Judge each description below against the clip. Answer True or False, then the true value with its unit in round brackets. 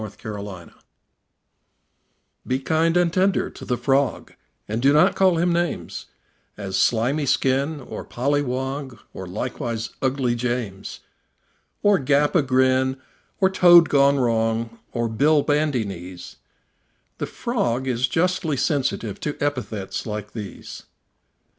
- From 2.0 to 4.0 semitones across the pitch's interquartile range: False (4.6 semitones)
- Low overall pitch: True (130 Hz)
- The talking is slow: True (130 wpm)